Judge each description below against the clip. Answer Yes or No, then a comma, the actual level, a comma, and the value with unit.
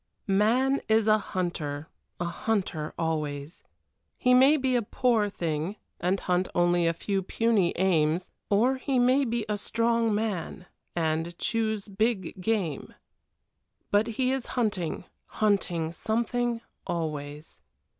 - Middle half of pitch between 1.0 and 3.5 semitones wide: No, average, 5.2 semitones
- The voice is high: Yes, high, 200 Hz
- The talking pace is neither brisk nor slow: No, slow, 130 wpm